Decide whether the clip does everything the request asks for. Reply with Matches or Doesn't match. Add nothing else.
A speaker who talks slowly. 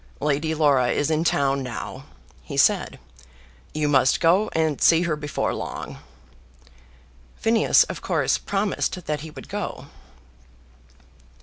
Matches